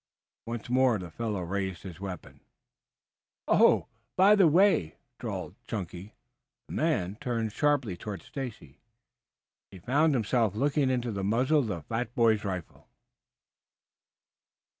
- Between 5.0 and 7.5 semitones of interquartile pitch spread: Yes, wide, 5.4 semitones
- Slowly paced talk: Yes, slow, 125 wpm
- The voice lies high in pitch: No, low, 110 Hz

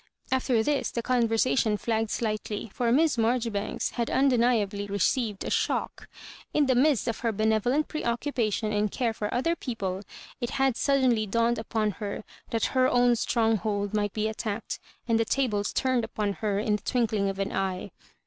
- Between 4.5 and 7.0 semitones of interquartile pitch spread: No, average, 2.8 semitones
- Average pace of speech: Yes, average, 170 wpm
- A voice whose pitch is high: Yes, high, 225 Hz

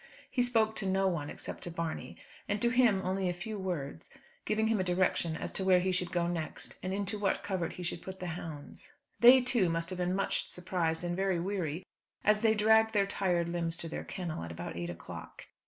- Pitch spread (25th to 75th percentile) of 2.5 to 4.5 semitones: Yes, average, 3.2 semitones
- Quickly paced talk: Yes, fast, 220 wpm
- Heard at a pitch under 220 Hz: Yes, medium, 185 Hz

